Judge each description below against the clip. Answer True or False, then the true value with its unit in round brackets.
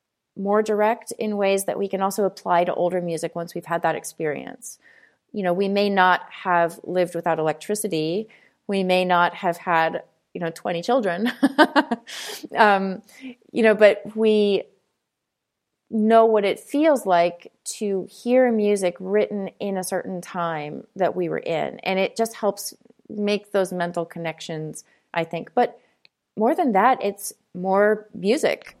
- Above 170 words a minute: False (155 wpm)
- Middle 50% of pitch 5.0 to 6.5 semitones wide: False (3.6 semitones)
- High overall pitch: True (195 Hz)